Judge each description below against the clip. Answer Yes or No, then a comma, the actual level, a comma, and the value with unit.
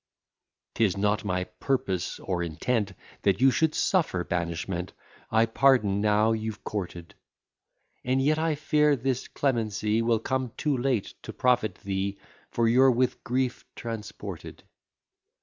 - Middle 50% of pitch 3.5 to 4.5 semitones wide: No, average, 4.9 semitones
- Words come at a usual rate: No, slow, 130 wpm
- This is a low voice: Yes, low, 115 Hz